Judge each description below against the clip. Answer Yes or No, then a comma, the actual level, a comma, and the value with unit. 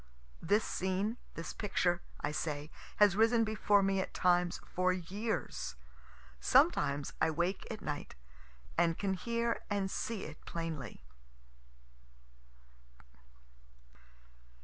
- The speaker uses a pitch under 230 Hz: Yes, medium, 185 Hz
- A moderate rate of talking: No, slow, 105 wpm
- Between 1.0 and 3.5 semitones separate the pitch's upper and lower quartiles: No, average, 3.9 semitones